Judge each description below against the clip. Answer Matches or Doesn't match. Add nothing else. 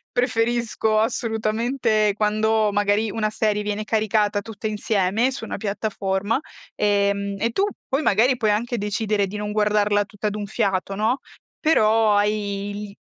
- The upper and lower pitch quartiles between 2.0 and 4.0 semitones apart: Doesn't match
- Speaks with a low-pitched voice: Doesn't match